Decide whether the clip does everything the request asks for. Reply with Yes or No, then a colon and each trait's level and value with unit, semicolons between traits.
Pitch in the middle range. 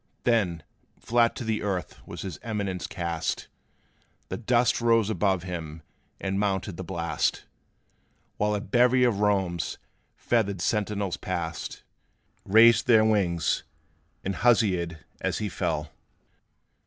No: low, 100 Hz